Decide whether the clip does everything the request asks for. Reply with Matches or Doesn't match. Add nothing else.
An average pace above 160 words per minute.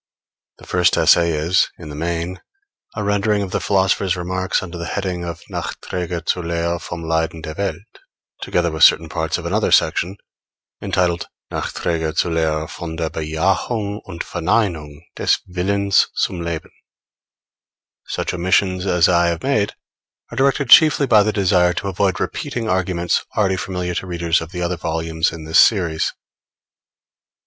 Doesn't match